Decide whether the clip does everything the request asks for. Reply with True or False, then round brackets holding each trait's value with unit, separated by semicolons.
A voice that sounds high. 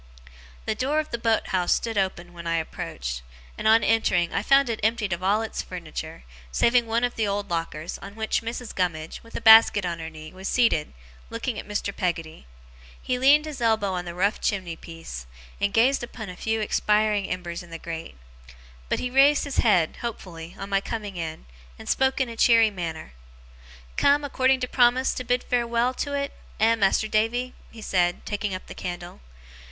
True (210 Hz)